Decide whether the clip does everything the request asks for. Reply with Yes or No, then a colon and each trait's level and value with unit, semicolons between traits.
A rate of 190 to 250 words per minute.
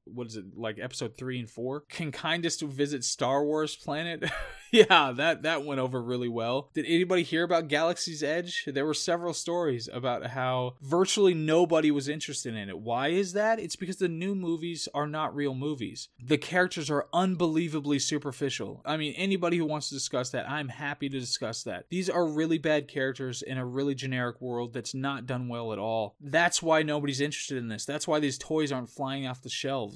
Yes: average, 200 wpm